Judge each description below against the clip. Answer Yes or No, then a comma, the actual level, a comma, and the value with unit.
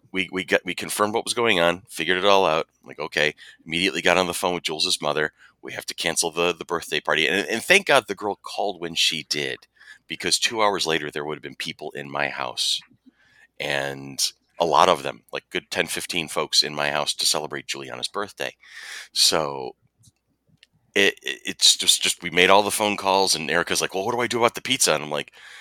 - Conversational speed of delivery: No, fast, 225 wpm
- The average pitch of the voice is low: Yes, very low, 90 Hz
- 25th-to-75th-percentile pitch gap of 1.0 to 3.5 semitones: No, average, 4.5 semitones